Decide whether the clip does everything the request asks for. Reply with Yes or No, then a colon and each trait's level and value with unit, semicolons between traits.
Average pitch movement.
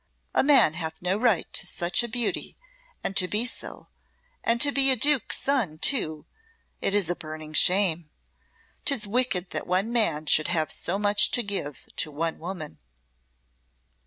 No: wide, 6.7 semitones